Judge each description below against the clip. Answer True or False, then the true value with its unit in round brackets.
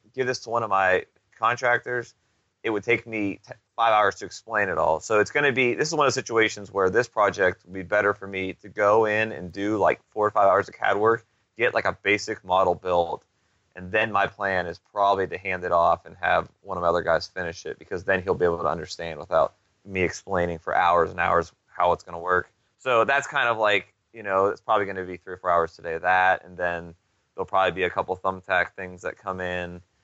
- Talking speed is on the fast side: True (250 wpm)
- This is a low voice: True (95 Hz)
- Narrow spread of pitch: False (3.2 semitones)